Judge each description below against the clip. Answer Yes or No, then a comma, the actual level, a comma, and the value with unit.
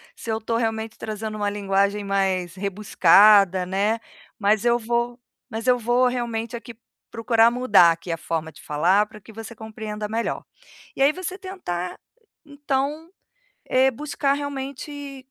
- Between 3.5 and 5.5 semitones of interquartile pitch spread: Yes, average, 4.1 semitones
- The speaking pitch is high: Yes, high, 225 Hz